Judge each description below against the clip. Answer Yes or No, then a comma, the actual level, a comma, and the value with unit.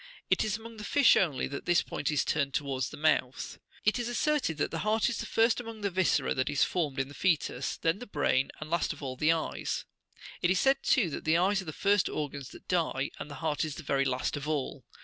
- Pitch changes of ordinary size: No, wide, 6.3 semitones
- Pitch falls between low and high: Yes, medium, 160 Hz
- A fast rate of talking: Yes, fast, 245 wpm